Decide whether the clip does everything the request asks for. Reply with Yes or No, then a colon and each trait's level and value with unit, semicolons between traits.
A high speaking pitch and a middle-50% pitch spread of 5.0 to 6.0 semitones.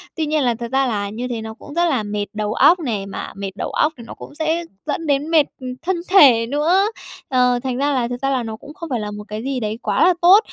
Yes: very high, 255 Hz; wide, 5.6 semitones